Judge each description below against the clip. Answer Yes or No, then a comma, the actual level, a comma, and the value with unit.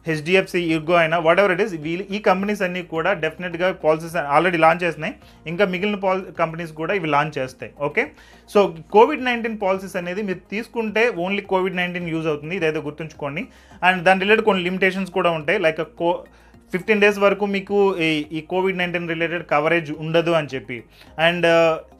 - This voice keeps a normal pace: No, fast, 170 wpm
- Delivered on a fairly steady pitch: No, average, 3.2 semitones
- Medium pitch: Yes, medium, 175 Hz